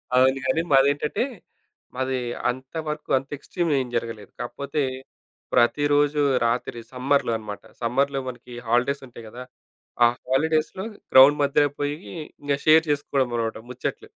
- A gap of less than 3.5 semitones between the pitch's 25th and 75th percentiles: Yes, average, 2.9 semitones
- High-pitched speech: No, low, 135 Hz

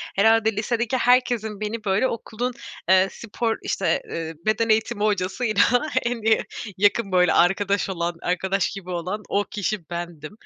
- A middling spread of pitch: Yes, average, 3.3 semitones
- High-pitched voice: Yes, high, 205 Hz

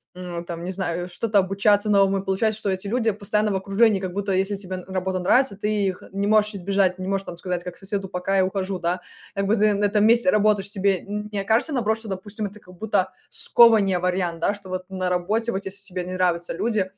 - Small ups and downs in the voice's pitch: Yes, narrow, 2.1 semitones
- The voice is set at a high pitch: Yes, high, 195 Hz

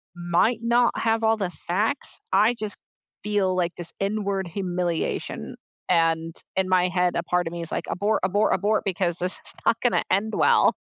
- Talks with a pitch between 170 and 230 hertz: Yes, high, 190 Hz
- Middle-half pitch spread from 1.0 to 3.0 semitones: No, average, 3.4 semitones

